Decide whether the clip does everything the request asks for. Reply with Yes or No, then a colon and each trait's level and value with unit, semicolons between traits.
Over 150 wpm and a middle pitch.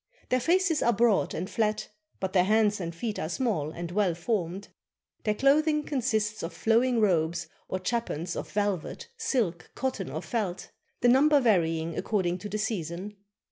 No: average, 170 wpm; high, 210 Hz